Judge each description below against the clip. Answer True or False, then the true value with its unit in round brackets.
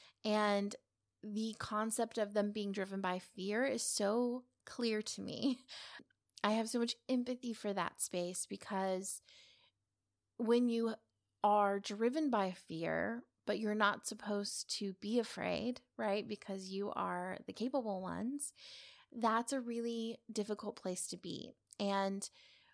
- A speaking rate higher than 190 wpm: False (135 wpm)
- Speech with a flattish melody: False (3.1 semitones)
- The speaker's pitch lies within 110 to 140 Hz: False (210 Hz)